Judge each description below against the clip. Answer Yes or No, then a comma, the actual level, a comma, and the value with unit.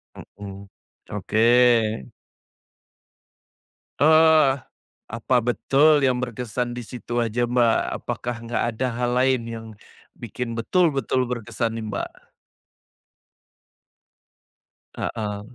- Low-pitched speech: Yes, low, 120 Hz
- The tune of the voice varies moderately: No, narrow, 2.1 semitones